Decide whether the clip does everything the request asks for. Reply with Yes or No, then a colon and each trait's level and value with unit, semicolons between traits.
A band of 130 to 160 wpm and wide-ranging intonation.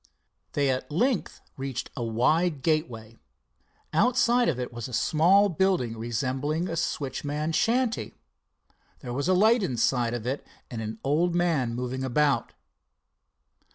Yes: slow, 135 wpm; wide, 6.1 semitones